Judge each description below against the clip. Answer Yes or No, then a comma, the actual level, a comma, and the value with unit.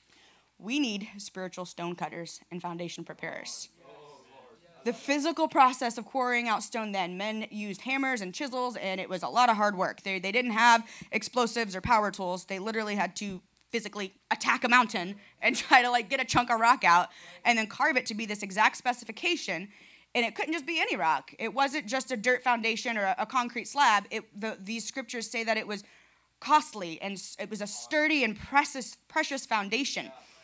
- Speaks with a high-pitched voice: Yes, high, 225 Hz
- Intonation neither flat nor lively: Yes, average, 4.2 semitones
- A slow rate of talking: No, average, 195 wpm